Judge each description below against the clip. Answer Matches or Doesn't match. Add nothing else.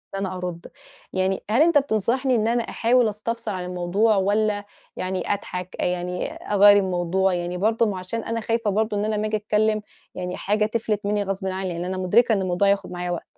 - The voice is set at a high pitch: Matches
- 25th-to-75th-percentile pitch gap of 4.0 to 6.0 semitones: Doesn't match